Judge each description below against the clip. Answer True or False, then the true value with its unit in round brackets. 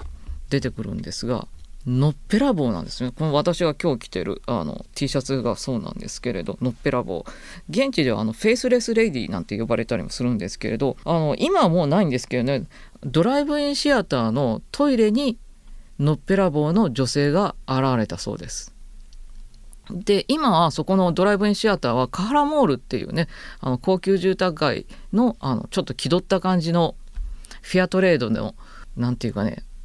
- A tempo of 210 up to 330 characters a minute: False (360 characters per minute)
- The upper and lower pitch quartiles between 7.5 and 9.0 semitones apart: True (8.1 semitones)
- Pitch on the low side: False (155 Hz)